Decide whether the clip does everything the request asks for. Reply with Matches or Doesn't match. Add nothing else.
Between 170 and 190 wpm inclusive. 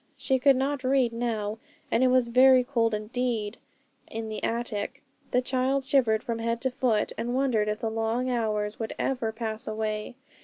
Matches